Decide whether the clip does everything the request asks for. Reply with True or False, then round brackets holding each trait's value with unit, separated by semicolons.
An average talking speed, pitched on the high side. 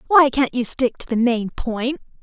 False (215 wpm; 255 Hz)